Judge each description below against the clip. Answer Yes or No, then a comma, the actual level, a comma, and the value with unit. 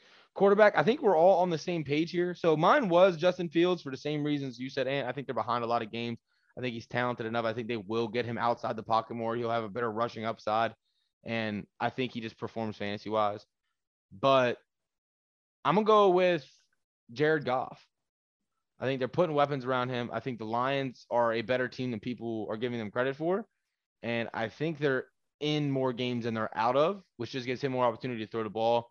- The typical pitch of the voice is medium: No, low, 125 Hz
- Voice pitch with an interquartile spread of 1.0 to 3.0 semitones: No, average, 4.4 semitones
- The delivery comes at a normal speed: No, fast, 225 wpm